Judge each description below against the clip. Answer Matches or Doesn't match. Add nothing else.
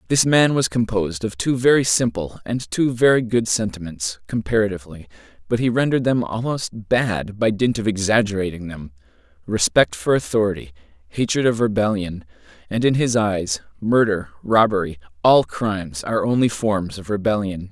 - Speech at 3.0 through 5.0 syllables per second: Doesn't match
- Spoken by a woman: Doesn't match